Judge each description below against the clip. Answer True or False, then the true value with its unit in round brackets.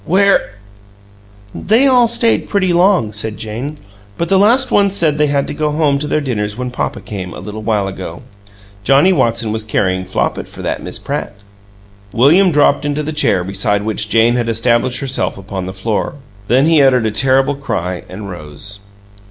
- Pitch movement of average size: False (6.7 semitones)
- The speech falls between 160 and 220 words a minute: True (185 wpm)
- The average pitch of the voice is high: False (120 Hz)